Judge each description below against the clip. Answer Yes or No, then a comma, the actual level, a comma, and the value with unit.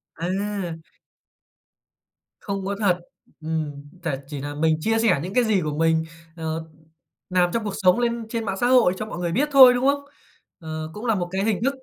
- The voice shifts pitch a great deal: Yes, wide, 5.7 semitones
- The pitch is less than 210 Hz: Yes, high, 190 Hz